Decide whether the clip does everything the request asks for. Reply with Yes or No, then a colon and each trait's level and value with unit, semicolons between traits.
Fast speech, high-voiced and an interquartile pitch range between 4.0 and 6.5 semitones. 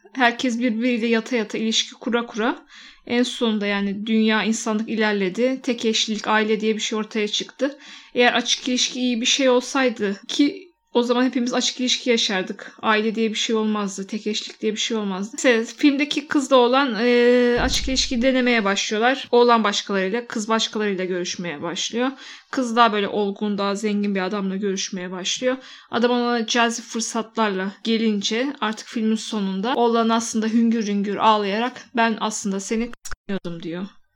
No: fast, 155 wpm; high, 230 Hz; average, 2.8 semitones